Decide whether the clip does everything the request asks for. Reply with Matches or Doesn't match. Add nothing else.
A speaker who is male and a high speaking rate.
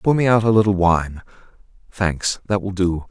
Doesn't match